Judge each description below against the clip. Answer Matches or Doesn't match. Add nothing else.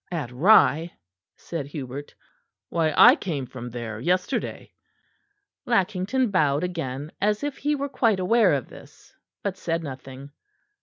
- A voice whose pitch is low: Doesn't match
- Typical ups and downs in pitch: Doesn't match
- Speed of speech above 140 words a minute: Doesn't match